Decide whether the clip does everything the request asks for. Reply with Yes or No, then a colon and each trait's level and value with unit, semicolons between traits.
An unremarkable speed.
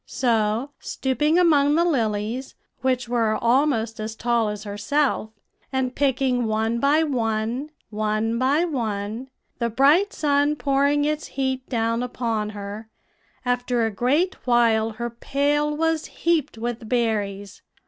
No: slow, 130 wpm